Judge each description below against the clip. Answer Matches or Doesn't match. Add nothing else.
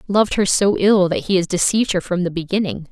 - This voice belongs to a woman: Matches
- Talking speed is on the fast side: Matches